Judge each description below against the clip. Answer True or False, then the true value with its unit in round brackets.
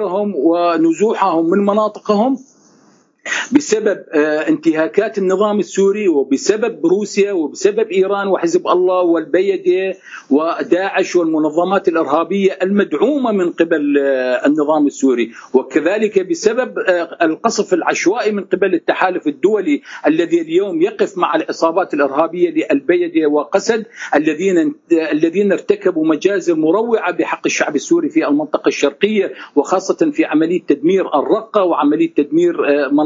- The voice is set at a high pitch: True (195 Hz)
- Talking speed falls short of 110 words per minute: True (100 wpm)